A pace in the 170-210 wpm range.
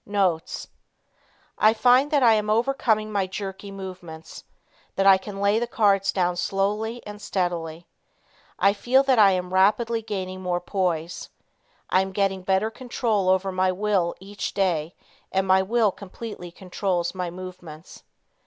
No: average, 150 wpm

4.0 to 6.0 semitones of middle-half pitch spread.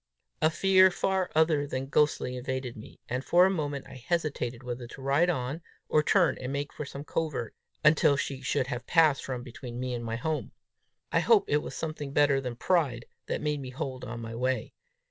No: average, 3.6 semitones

